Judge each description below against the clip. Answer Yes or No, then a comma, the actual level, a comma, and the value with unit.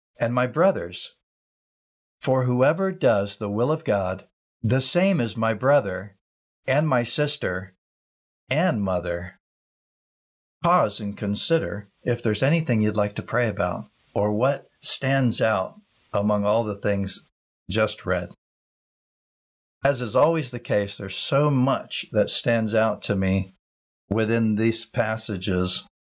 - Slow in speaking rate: Yes, slow, 130 wpm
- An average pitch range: Yes, average, 4.4 semitones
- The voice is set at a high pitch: No, low, 110 Hz